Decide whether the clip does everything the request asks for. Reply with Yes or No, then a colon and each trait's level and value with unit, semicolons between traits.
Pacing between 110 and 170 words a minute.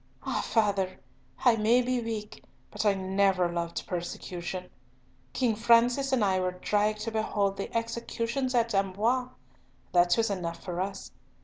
Yes: average, 145 wpm